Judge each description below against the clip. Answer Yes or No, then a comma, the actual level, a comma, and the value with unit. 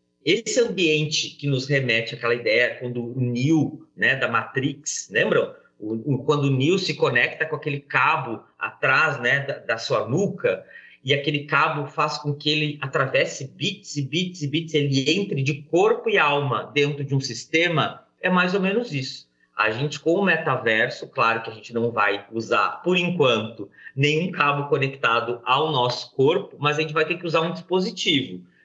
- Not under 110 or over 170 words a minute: No, average, 180 wpm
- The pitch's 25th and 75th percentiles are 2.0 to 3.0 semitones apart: No, average, 4.0 semitones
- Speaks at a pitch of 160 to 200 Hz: No, medium, 150 Hz